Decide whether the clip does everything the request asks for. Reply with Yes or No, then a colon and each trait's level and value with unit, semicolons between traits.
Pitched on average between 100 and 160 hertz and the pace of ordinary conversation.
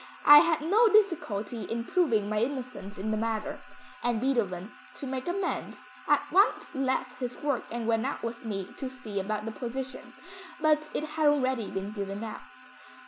No: very high, 250 Hz; average, 175 wpm